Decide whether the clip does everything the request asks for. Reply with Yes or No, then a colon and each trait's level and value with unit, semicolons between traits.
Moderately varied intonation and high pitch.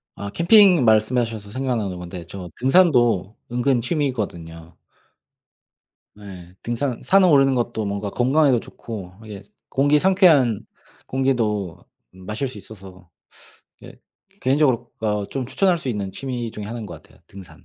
No: average, 5.0 semitones; low, 115 Hz